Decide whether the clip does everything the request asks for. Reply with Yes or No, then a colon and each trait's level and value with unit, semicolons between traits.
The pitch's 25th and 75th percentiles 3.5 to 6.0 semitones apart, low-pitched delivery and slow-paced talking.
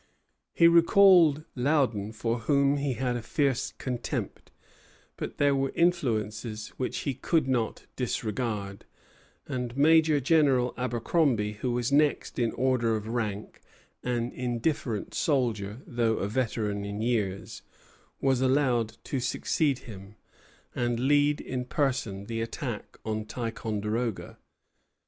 Yes: average, 3.9 semitones; low, 125 Hz; slow, 120 wpm